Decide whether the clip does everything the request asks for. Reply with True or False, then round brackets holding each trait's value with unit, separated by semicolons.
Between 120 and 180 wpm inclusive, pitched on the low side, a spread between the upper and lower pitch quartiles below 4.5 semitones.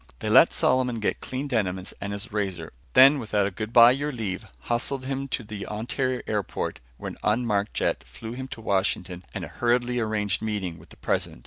False (195 wpm; 110 Hz; 3.7 semitones)